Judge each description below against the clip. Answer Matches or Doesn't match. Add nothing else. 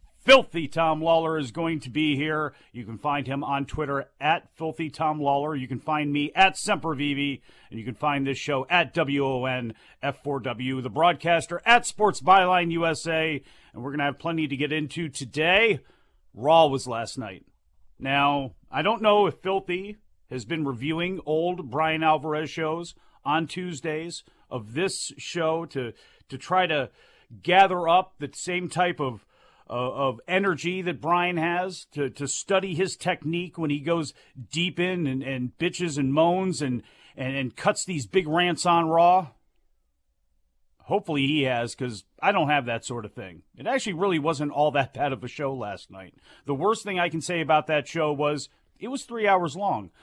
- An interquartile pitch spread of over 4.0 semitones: Matches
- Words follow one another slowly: Doesn't match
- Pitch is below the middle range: Doesn't match